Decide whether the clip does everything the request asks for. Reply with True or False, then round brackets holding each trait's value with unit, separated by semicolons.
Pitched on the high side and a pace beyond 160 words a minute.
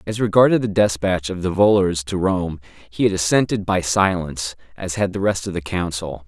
False (95 Hz; 200 wpm)